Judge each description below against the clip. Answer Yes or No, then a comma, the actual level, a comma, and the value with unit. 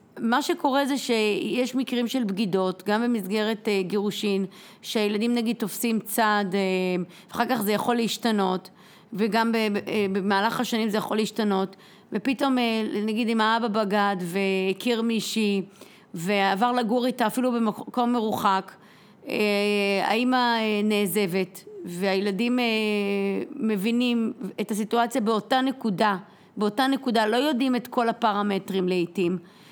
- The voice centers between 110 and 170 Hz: No, high, 215 Hz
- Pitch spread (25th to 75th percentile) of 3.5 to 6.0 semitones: No, average, 3.0 semitones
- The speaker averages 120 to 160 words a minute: Yes, average, 125 wpm